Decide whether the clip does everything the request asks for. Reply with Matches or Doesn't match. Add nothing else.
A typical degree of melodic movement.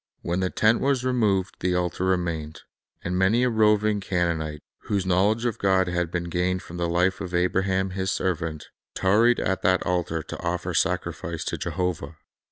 Doesn't match